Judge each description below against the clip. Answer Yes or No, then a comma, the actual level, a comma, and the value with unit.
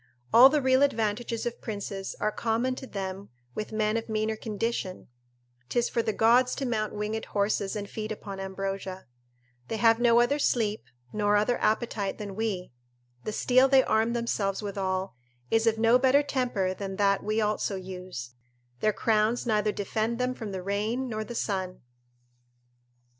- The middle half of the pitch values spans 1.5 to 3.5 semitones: Yes, average, 2.9 semitones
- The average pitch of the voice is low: No, high, 215 Hz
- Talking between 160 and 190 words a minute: Yes, average, 165 wpm